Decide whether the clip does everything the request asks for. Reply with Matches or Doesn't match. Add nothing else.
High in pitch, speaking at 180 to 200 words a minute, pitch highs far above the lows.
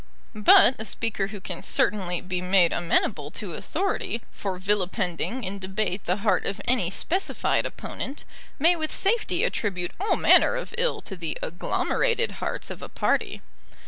Doesn't match